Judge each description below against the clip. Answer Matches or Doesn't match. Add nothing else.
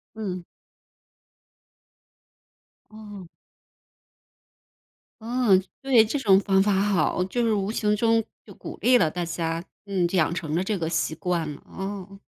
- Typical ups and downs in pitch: Matches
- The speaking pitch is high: Matches